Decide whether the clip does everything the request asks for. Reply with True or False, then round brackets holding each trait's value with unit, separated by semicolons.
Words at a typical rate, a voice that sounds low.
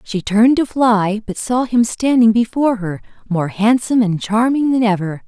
False (180 wpm; 220 Hz)